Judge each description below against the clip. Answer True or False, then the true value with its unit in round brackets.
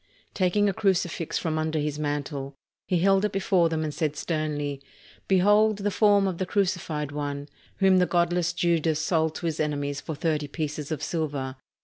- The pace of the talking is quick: False (175 wpm)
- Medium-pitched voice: True (160 Hz)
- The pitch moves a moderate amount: True (3.8 semitones)